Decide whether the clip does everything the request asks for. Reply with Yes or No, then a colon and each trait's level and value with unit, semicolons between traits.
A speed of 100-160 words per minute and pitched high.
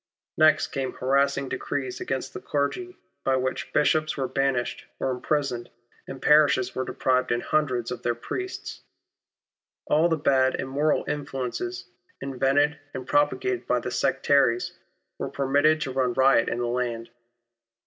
No: average, 140 wpm; low, 135 Hz